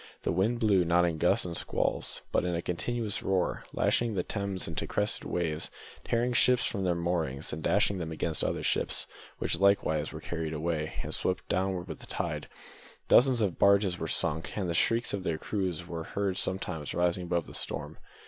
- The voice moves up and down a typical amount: Yes, average, 3.2 semitones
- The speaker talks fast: No, average, 195 wpm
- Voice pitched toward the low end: Yes, very low, 90 Hz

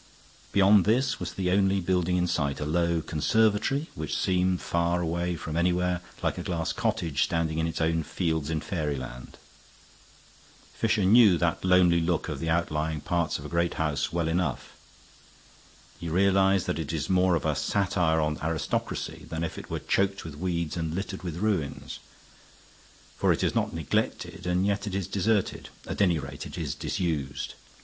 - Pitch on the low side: Yes, very low, 85 Hz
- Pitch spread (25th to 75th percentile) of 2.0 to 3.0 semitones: Yes, average, 2.7 semitones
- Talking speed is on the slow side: No, average, 175 wpm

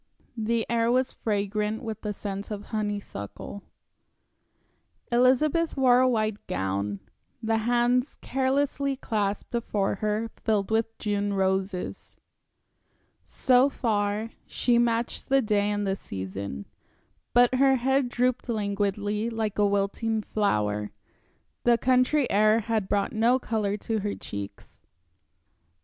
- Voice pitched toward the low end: No, high, 220 Hz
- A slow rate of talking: Yes, slow, 125 wpm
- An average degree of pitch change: Yes, average, 3.2 semitones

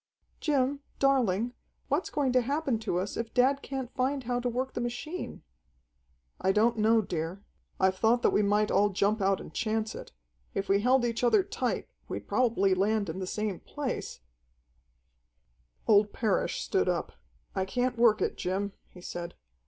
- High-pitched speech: Yes, high, 220 Hz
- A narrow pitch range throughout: No, average, 4.6 semitones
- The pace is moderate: Yes, average, 175 wpm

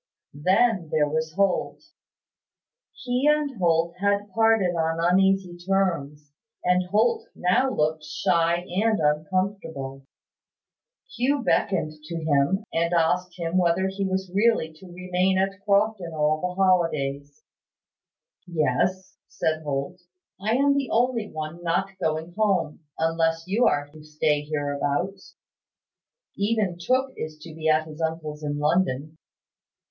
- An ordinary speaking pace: No, slow, 130 wpm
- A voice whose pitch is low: No, medium, 175 Hz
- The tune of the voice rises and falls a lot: No, average, 3.9 semitones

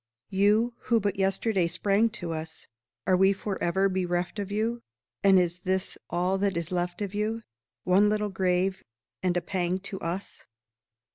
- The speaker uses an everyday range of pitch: No, narrow, 2.3 semitones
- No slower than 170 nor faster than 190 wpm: No, average, 160 wpm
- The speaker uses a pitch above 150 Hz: Yes, high, 190 Hz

